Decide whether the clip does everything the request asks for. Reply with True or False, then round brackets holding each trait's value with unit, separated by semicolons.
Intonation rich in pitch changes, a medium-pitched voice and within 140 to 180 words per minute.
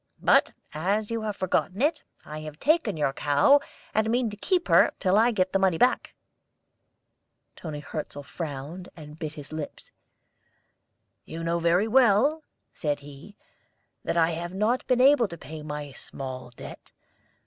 True (6.4 semitones; 175 Hz; 160 wpm)